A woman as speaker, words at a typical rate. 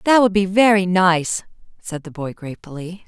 Yes: female; average, 175 wpm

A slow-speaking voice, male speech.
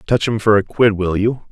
No: fast, 280 wpm; male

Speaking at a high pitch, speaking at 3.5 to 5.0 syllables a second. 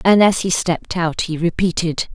No: medium, 175 Hz; 4.9 syllables/s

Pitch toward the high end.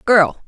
Yes: high, 195 Hz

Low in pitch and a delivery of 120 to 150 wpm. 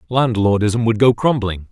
Yes: low, 110 Hz; average, 140 wpm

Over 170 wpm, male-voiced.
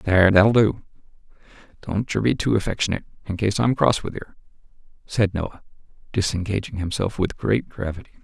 No: average, 155 wpm; male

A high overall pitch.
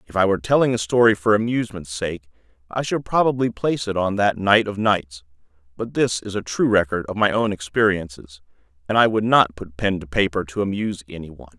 No: low, 100 Hz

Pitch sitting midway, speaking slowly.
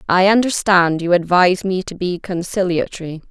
Yes: medium, 180 Hz; slow, 125 wpm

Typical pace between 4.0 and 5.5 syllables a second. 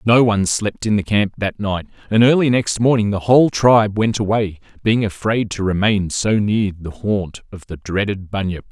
Yes: 4.9 syllables/s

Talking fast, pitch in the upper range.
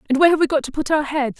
Yes: fast, 390 wpm; very high, 290 Hz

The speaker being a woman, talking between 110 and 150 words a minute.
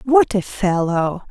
Yes: female; average, 140 wpm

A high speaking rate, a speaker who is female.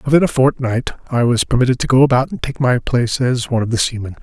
No: fast, 255 wpm; male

